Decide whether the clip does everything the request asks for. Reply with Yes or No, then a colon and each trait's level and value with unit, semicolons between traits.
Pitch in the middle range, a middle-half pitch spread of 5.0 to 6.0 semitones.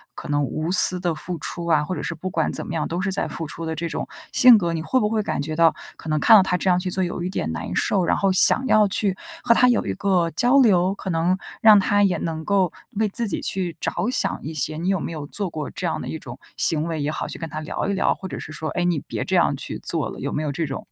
No: medium, 175 Hz; average, 3.6 semitones